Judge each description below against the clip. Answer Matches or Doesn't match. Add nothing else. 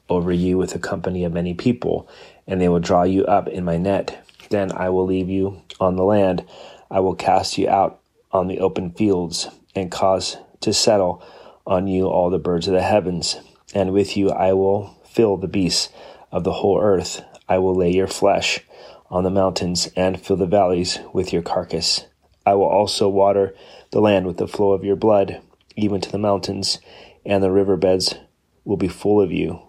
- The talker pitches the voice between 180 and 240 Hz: Doesn't match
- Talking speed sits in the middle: Matches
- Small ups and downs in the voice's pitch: Matches